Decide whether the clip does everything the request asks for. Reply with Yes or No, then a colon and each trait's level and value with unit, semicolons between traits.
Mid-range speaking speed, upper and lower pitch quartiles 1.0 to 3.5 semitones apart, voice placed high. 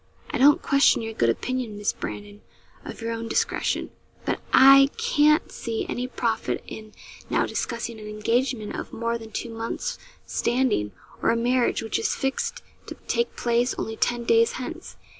Yes: average, 165 wpm; average, 3.2 semitones; high, 235 Hz